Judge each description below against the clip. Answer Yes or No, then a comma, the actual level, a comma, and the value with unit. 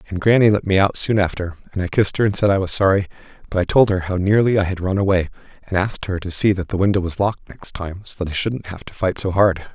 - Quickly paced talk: Yes, fast, 290 wpm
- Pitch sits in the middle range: No, very low, 95 Hz